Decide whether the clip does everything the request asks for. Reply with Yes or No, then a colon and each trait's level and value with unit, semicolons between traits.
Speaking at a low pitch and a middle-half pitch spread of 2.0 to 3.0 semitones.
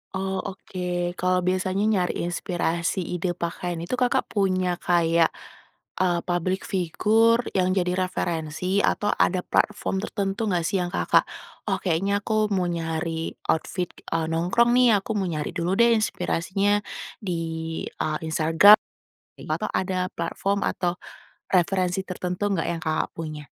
No: medium, 180 Hz; narrow, 2.4 semitones